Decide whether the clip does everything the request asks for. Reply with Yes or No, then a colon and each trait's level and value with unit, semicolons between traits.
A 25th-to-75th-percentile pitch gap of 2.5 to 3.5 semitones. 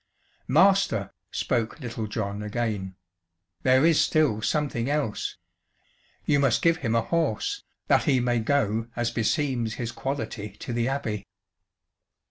No: average, 4.5 semitones